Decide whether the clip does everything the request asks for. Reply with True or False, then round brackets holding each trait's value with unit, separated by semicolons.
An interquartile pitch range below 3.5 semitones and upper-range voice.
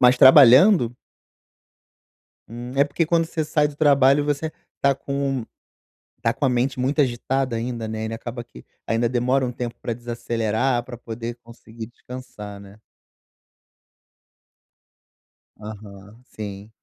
False (3.1 semitones; 120 Hz)